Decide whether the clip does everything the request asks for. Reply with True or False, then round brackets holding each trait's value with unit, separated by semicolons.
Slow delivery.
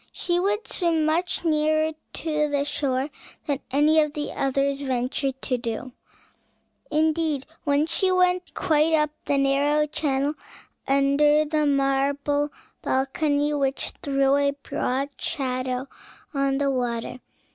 True (125 wpm)